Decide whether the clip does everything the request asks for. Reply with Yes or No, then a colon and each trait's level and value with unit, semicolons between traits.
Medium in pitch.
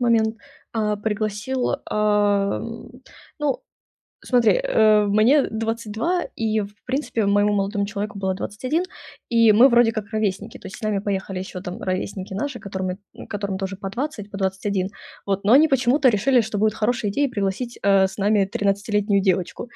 No: high, 210 Hz